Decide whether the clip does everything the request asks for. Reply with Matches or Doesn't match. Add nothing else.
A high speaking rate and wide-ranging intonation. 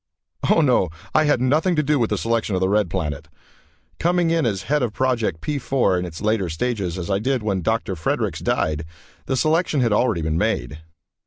Matches